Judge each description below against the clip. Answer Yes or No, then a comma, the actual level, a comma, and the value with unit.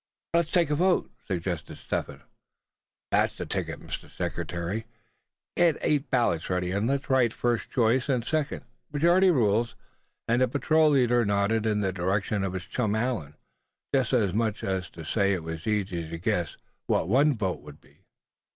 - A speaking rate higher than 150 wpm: Yes, average, 170 wpm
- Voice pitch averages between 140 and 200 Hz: No, low, 110 Hz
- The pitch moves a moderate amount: No, wide, 6.1 semitones